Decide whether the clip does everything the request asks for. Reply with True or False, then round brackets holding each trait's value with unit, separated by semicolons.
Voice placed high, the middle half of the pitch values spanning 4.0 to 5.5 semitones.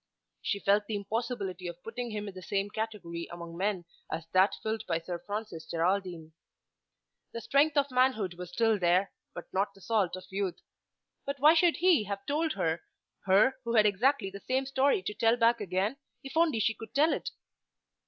True (205 Hz; 4.9 semitones)